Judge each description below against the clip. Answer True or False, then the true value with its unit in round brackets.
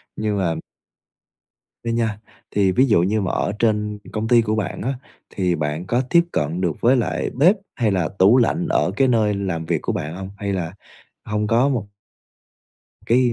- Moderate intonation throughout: True (4.2 semitones)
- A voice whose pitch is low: True (105 Hz)